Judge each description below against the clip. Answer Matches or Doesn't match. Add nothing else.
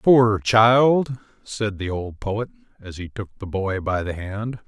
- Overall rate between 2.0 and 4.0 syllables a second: Matches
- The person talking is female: Doesn't match